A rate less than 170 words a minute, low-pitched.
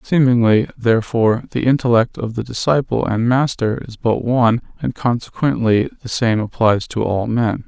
Yes: average, 155 wpm; low, 120 Hz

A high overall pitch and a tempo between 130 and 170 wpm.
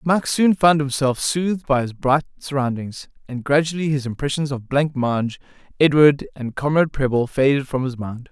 No: medium, 140 Hz; average, 165 wpm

